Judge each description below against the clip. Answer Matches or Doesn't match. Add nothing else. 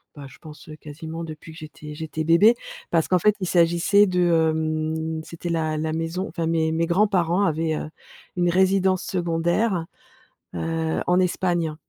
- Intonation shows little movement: Matches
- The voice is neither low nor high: Matches